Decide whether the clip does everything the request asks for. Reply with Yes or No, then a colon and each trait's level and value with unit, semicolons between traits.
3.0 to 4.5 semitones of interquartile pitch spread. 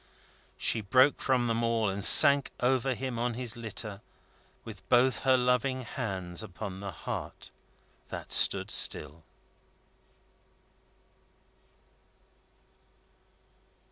Yes: average, 4.1 semitones